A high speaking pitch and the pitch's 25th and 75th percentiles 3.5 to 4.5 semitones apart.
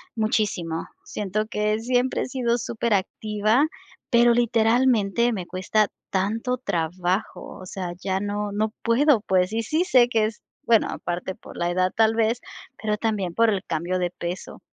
Yes: high, 215 Hz; average, 3.8 semitones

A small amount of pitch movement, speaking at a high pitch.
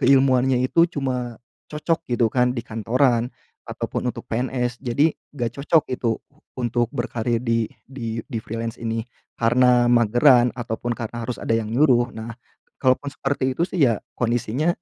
No: narrow, 2.1 semitones; low, 120 Hz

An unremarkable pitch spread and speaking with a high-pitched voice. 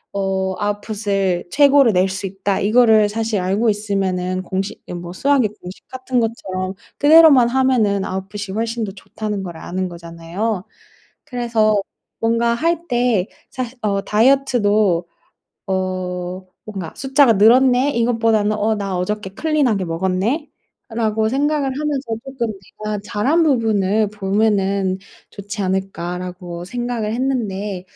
Yes: average, 4.0 semitones; high, 210 Hz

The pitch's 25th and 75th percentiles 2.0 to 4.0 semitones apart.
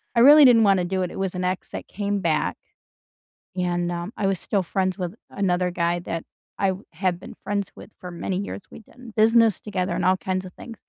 Yes: narrow, 2.4 semitones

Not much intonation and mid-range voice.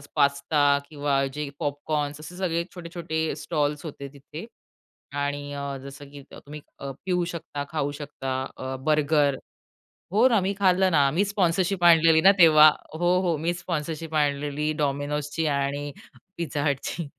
No: average, 3.0 semitones; medium, 150 Hz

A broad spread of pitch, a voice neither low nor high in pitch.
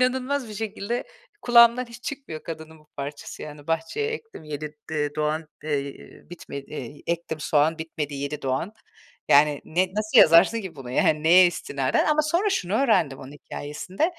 Yes: wide, 7.4 semitones; medium, 160 Hz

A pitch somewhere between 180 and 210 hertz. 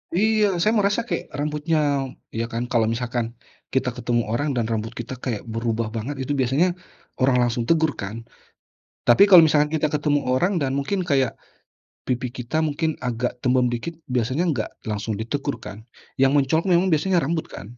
No: low, 130 Hz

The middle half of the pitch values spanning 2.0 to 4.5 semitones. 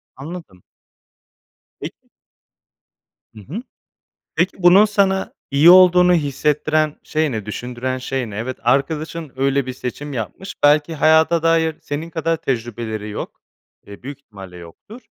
No: average, 5.1 semitones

